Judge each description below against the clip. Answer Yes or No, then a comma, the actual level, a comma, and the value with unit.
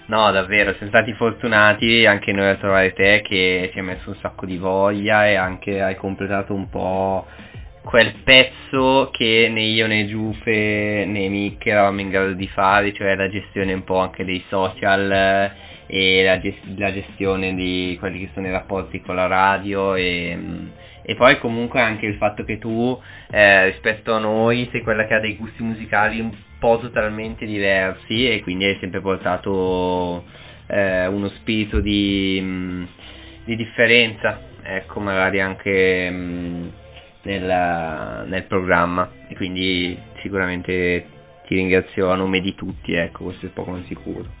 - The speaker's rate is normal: Yes, average, 155 wpm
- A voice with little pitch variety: Yes, narrow, 2.3 semitones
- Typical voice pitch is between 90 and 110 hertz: Yes, very low, 95 Hz